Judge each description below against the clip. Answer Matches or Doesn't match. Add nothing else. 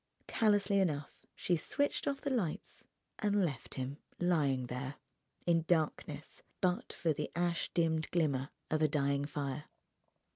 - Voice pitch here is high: Doesn't match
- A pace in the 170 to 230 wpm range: Doesn't match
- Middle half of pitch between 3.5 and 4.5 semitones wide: Matches